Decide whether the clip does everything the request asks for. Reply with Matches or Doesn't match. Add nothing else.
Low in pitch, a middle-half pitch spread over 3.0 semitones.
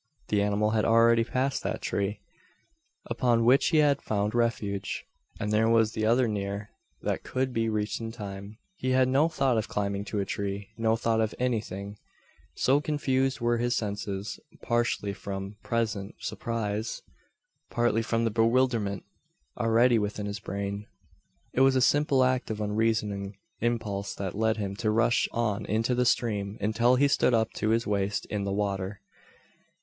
Doesn't match